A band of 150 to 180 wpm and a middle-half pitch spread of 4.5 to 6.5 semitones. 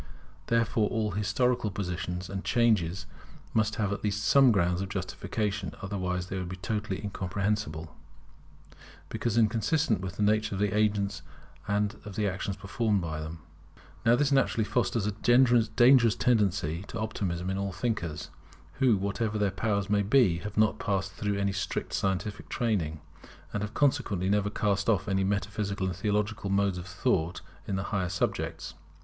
No: average, 160 wpm; narrow, 2.4 semitones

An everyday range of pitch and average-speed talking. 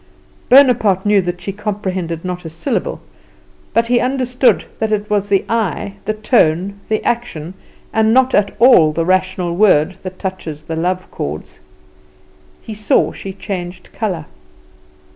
Yes: average, 3.8 semitones; average, 145 wpm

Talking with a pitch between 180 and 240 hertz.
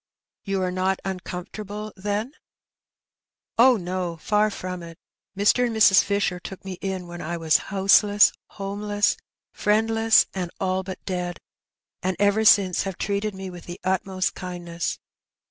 Yes: high, 190 Hz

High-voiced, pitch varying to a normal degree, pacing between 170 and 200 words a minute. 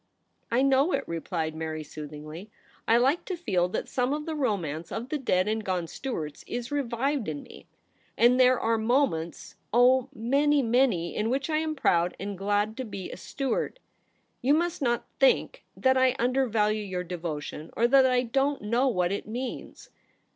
No: high, 235 Hz; wide, 6.7 semitones; average, 190 wpm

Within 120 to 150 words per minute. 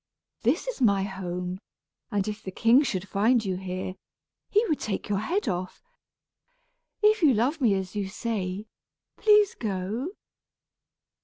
Yes: average, 145 wpm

